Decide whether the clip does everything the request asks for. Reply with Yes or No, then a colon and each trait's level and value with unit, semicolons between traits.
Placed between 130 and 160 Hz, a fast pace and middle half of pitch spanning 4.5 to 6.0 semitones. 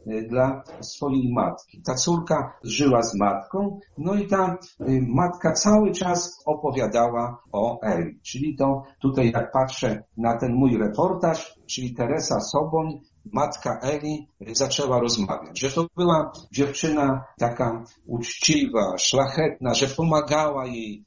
No: low, 135 Hz; average, 125 wpm; average, 4.8 semitones